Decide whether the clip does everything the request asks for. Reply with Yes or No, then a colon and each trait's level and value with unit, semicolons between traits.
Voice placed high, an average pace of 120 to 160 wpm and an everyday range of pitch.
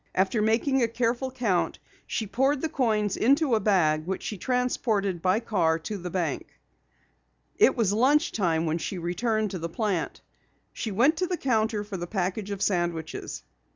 No: high, 210 Hz; average, 175 wpm; average, 4.9 semitones